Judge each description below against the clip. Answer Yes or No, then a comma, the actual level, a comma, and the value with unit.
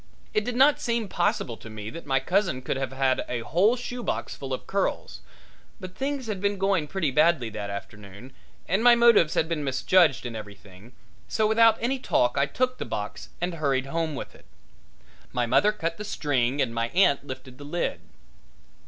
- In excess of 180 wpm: Yes, average, 190 wpm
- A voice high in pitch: No, medium, 155 Hz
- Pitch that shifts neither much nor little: No, wide, 8.2 semitones